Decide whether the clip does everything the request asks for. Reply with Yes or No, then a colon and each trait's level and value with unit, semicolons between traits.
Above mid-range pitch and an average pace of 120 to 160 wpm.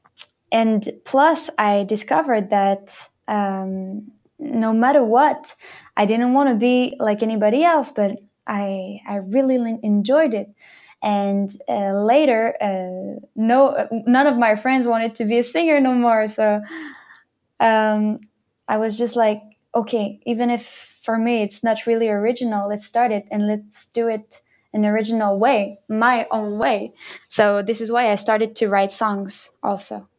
Yes: high, 220 Hz; average, 155 wpm